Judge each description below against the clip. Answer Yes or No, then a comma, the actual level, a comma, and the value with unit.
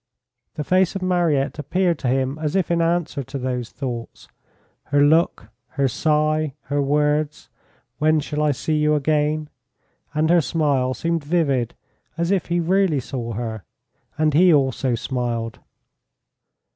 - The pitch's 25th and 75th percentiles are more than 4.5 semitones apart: No, average, 3.6 semitones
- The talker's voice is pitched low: No, medium, 150 Hz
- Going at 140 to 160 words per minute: Yes, average, 145 wpm